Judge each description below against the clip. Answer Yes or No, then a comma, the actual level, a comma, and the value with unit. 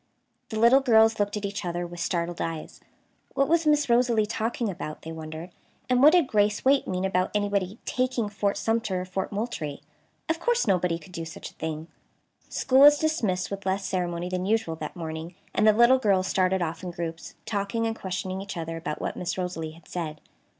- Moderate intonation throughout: Yes, average, 4.7 semitones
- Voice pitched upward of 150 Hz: Yes, high, 190 Hz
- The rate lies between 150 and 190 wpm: No, average, 200 wpm